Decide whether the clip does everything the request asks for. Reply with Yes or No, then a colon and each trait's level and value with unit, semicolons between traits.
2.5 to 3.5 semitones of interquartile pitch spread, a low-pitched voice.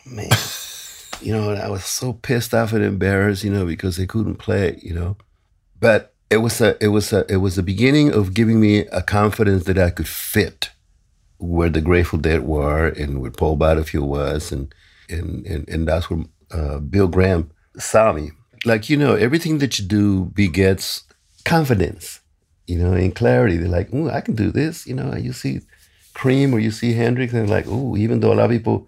No: average, 5.0 semitones; low, 100 Hz